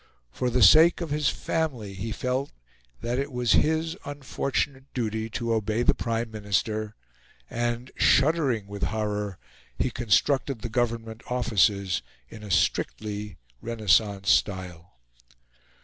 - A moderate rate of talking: No, slow, 125 wpm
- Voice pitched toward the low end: Yes, low, 115 Hz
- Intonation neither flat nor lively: Yes, average, 3.7 semitones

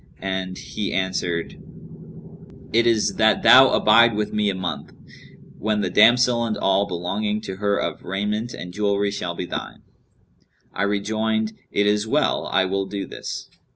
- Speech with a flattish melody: Yes, narrow, 2.3 semitones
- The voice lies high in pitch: No, low, 105 Hz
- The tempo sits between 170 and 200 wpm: No, average, 155 wpm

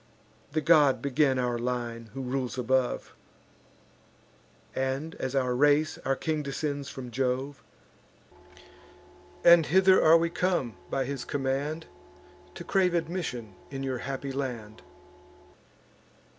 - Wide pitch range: No, average, 3.5 semitones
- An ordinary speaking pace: No, slow, 115 wpm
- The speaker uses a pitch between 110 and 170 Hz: Yes, low, 135 Hz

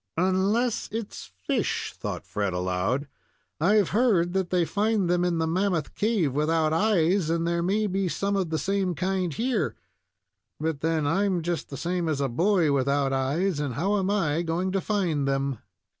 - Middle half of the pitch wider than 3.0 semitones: Yes, average, 4.5 semitones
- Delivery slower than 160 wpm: No, average, 175 wpm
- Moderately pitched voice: Yes, medium, 175 Hz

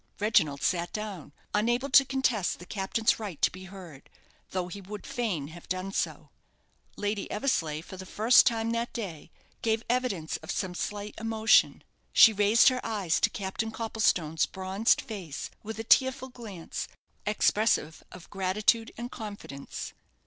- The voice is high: Yes, high, 205 Hz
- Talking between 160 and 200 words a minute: No, average, 150 wpm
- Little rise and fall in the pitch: No, average, 3.6 semitones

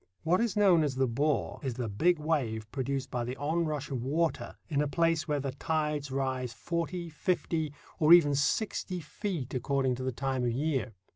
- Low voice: No, medium, 145 Hz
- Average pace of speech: Yes, average, 190 wpm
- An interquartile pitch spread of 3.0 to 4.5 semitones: Yes, average, 3.9 semitones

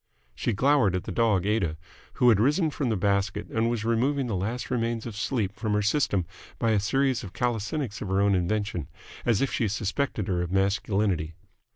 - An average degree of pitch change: Yes, average, 3.7 semitones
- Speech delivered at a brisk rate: No, average, 195 wpm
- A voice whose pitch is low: Yes, low, 105 Hz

